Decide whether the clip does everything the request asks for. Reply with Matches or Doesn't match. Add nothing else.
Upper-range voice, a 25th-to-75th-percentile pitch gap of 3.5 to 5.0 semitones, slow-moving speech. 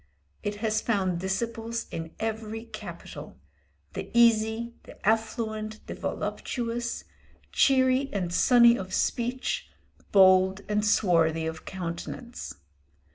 Matches